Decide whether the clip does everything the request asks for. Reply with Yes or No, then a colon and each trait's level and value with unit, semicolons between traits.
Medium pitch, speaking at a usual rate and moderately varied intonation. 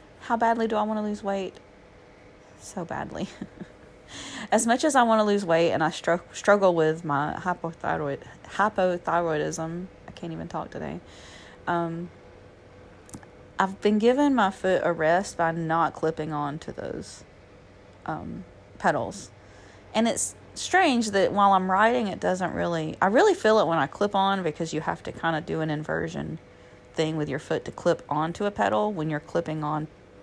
Yes: medium, 170 Hz; average, 175 wpm; average, 4.8 semitones